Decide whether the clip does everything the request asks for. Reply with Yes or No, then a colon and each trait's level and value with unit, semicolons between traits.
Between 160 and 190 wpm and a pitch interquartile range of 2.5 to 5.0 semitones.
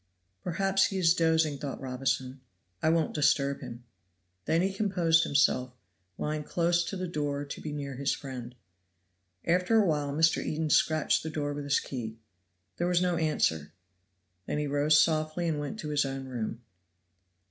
Yes: average, 170 wpm; average, 3.2 semitones